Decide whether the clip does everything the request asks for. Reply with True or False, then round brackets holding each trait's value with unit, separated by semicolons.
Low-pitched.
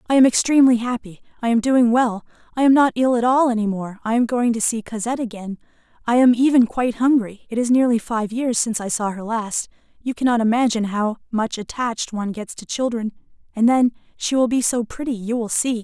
False (235 Hz)